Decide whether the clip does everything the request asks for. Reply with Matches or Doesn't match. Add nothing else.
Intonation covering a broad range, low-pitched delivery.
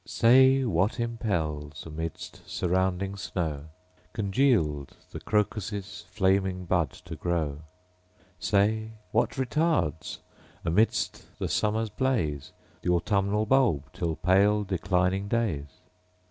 Doesn't match